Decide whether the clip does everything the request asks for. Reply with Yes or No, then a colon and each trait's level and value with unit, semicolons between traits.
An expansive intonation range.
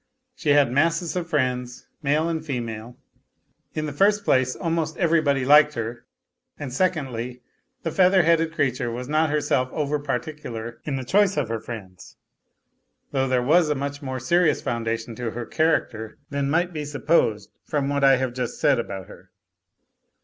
No: average, 4.4 semitones